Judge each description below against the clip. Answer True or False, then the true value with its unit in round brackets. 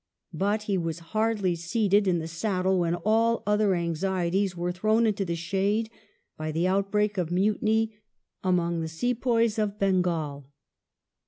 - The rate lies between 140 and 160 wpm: True (145 wpm)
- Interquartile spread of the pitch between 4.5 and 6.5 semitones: False (3.8 semitones)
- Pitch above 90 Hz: True (190 Hz)